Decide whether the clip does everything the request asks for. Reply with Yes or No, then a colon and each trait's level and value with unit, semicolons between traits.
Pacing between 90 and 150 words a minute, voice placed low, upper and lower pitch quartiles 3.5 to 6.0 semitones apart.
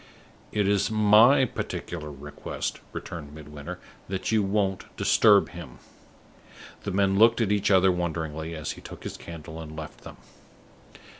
Yes: average, 145 wpm; very low, 95 Hz; average, 4.5 semitones